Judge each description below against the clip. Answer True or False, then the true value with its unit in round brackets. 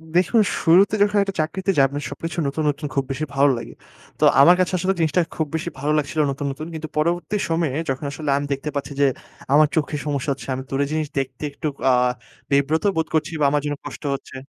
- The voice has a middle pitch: True (155 Hz)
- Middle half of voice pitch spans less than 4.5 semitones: True (2.7 semitones)